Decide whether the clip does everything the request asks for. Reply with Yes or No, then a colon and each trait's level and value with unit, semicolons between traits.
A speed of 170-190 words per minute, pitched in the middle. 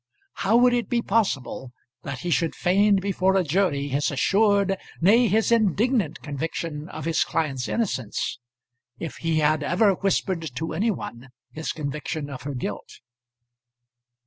No: average, 145 wpm; medium, 165 Hz